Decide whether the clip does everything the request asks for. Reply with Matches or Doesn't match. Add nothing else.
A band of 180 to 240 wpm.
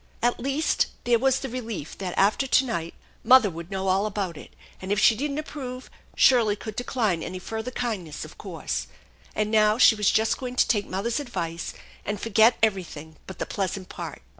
Matches